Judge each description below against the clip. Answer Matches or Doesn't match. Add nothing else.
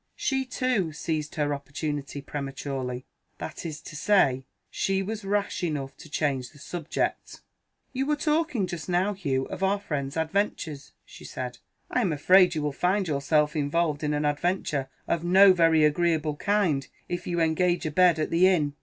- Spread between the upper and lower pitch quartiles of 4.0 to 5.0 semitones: Matches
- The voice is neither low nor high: Matches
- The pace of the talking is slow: Doesn't match